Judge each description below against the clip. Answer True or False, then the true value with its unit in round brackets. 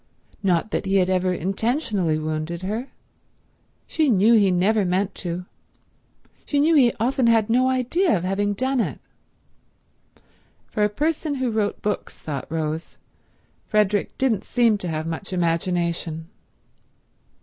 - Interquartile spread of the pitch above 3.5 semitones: True (5.1 semitones)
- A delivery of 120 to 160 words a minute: True (135 wpm)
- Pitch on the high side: True (200 Hz)